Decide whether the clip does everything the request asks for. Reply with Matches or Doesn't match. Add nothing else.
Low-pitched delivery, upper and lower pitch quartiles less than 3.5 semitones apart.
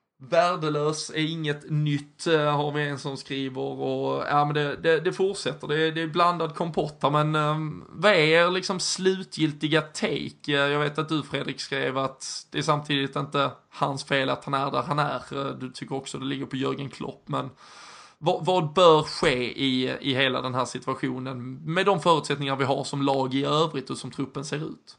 Doesn't match